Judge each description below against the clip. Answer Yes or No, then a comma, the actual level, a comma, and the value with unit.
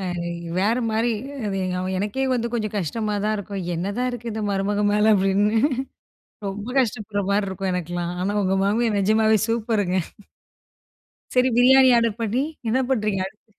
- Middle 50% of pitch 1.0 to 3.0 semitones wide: Yes, average, 2.7 semitones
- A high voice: Yes, high, 210 Hz